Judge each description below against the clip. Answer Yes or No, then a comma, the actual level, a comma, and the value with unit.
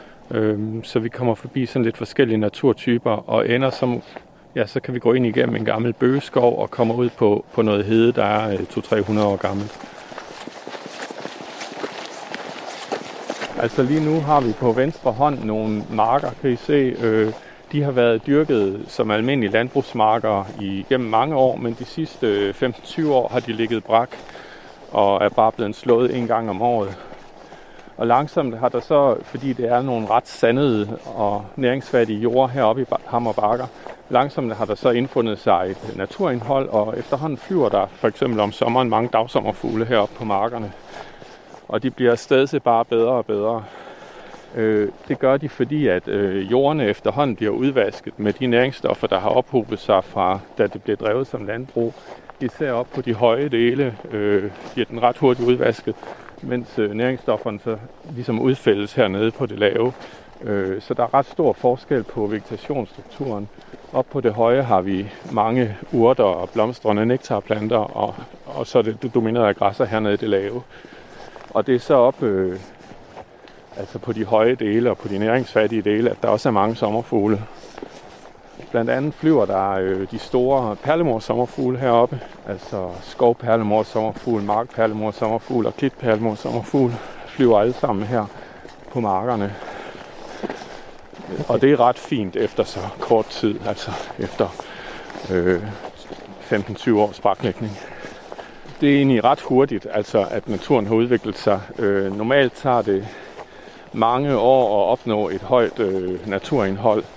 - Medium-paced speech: Yes, average, 155 wpm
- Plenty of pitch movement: No, average, 3.0 semitones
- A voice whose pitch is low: Yes, low, 115 Hz